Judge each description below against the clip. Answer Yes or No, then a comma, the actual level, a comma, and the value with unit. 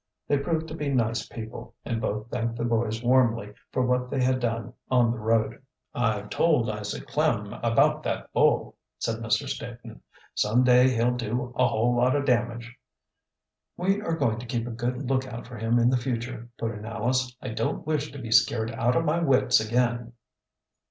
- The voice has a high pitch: No, low, 120 Hz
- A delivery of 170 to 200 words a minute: Yes, average, 190 wpm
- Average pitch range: No, narrow, 2.1 semitones